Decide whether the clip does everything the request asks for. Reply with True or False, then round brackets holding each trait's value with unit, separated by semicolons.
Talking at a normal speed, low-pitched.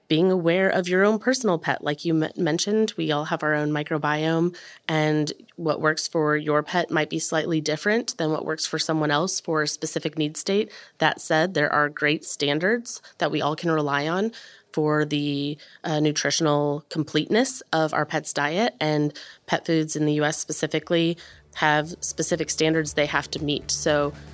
False (180 wpm; 155 Hz)